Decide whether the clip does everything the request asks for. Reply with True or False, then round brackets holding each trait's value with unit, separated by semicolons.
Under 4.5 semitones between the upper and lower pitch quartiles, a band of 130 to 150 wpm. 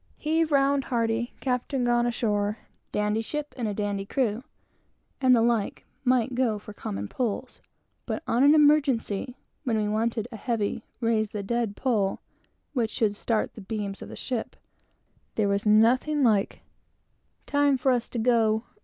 True (3.4 semitones; 140 wpm)